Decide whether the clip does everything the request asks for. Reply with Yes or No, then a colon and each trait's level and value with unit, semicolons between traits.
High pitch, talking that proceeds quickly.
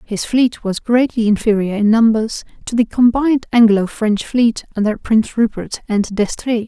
No: high, 225 Hz; average, 160 wpm